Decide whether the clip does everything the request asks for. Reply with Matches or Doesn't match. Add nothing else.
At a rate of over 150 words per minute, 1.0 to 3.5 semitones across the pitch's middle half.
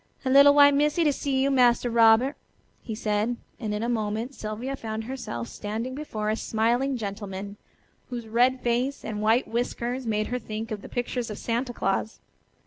Matches